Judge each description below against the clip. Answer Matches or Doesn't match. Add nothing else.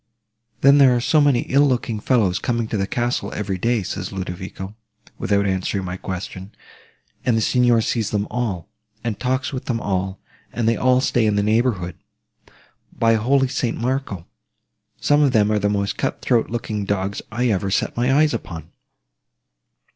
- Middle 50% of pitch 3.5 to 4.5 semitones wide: Matches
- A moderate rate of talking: Matches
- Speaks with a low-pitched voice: Matches